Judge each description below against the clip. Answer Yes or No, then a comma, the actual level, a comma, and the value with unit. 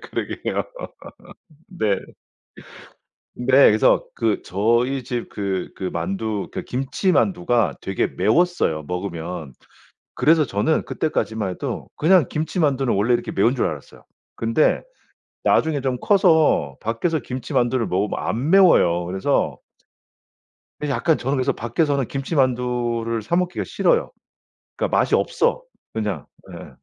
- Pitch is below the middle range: Yes, low, 120 Hz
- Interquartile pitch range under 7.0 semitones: Yes, wide, 6.6 semitones